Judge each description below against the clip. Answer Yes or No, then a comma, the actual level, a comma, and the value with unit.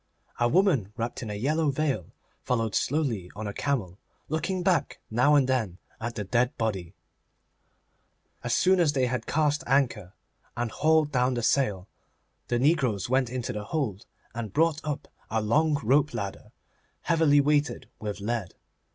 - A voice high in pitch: No, low, 125 Hz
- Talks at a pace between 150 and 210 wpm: Yes, average, 160 wpm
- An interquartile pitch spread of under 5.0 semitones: No, average, 5.3 semitones